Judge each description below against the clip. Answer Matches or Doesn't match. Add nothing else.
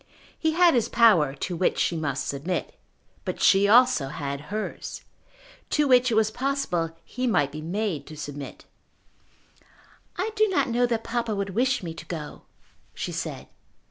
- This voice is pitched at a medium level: Doesn't match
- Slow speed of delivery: Doesn't match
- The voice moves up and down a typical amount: Doesn't match